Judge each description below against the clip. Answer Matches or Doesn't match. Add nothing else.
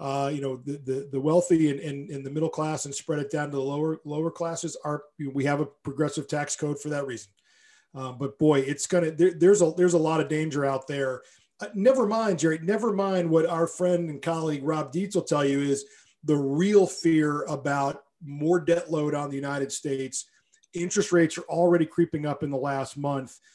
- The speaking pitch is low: Doesn't match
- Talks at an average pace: Doesn't match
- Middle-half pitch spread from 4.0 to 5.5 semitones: Doesn't match